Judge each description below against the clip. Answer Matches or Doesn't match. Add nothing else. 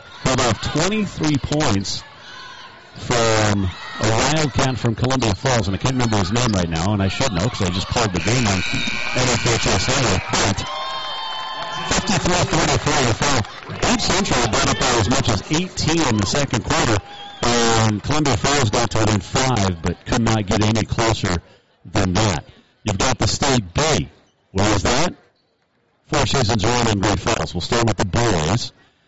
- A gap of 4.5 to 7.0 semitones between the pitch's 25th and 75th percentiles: Matches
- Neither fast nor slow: Matches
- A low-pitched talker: Matches